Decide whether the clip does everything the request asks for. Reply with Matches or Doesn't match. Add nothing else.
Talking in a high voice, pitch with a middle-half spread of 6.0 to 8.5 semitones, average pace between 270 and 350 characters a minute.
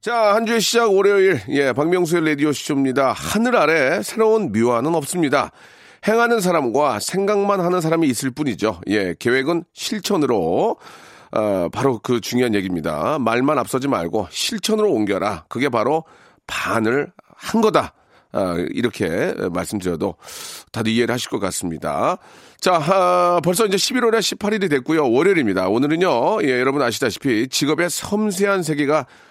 Doesn't match